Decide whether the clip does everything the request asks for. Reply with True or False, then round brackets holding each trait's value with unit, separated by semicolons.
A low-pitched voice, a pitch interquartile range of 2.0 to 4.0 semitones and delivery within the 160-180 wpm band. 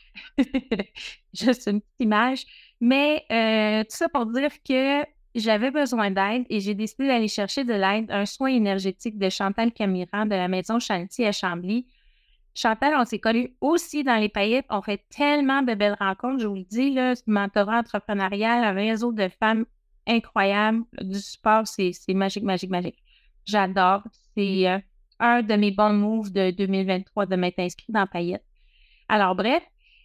False (215 Hz; 3.4 semitones; 165 wpm)